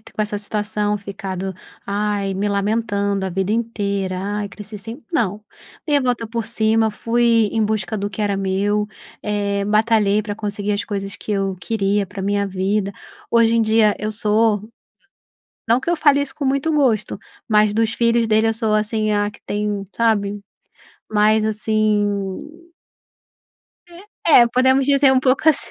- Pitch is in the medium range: No, high, 210 Hz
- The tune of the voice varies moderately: No, narrow, 2.2 semitones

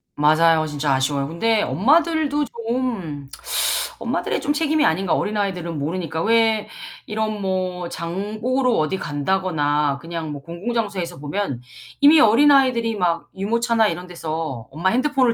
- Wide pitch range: Yes, wide, 6.5 semitones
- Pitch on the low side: No, high, 190 Hz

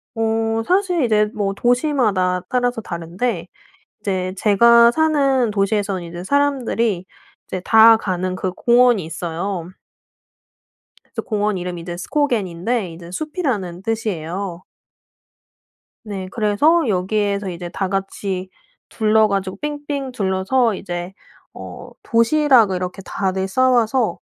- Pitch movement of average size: Yes, average, 4.7 semitones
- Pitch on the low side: No, high, 205 Hz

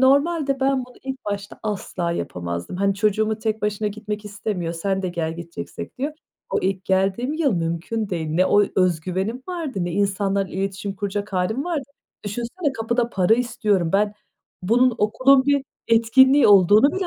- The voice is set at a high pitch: Yes, high, 210 Hz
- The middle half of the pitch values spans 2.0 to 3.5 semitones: No, average, 4.8 semitones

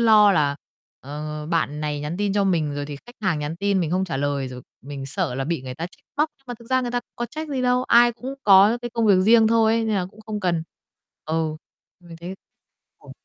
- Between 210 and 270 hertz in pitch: No, medium, 185 Hz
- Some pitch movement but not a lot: No, wide, 7.0 semitones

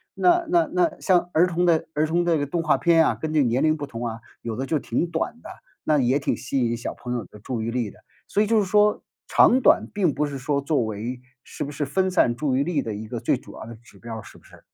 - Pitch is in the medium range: Yes, medium, 145 Hz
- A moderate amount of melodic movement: No, wide, 6.3 semitones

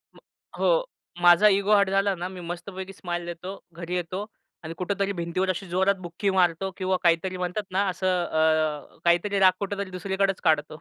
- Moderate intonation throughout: No, narrow, 2.2 semitones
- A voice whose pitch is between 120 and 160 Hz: No, medium, 185 Hz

